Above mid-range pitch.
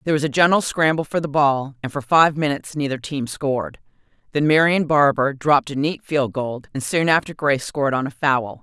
No: medium, 145 Hz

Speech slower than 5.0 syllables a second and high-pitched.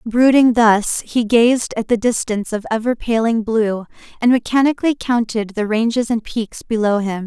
Yes: 4.7 syllables/s; high, 225 Hz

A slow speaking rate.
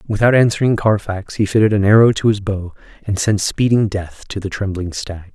No: average, 200 wpm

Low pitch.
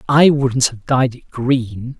Yes: low, 130 Hz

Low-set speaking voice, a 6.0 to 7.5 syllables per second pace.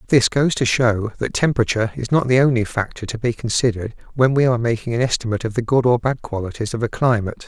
Yes: low, 120 Hz; 6.8 syllables/s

